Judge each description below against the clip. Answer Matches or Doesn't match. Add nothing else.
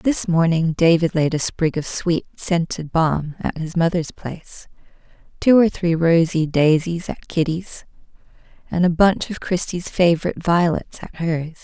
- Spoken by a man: Doesn't match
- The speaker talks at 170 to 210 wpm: Doesn't match